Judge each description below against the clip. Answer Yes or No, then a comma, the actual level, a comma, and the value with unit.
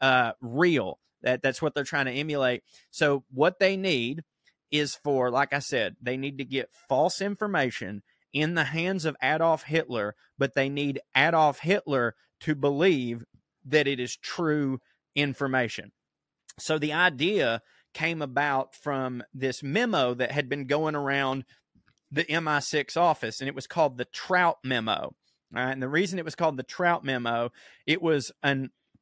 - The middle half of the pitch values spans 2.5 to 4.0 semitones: Yes, average, 3.3 semitones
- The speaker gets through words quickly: No, average, 165 wpm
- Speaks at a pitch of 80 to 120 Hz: No, medium, 140 Hz